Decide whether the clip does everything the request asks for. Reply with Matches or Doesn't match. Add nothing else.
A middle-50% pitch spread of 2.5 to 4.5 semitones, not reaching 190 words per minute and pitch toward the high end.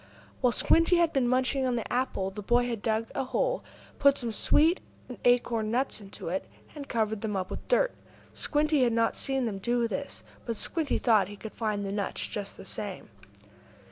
Doesn't match